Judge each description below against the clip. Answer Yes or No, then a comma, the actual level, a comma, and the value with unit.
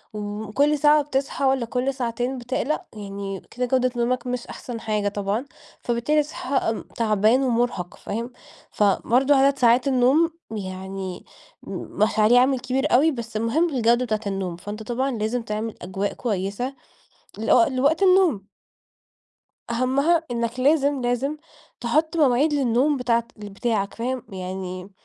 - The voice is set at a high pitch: Yes, high, 245 Hz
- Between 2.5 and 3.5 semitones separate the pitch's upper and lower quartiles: No, average, 4.1 semitones